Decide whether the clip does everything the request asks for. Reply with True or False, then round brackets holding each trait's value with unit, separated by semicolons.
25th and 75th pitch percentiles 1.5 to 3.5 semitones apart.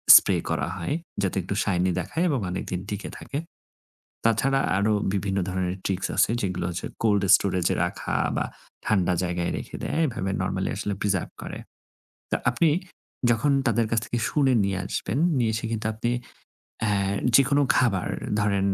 False (4.1 semitones)